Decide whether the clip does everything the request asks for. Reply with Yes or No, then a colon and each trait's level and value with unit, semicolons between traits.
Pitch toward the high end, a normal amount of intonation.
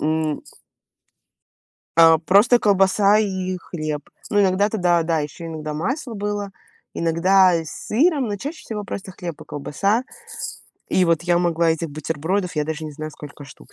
No: medium, 175 Hz; average, 4.3 semitones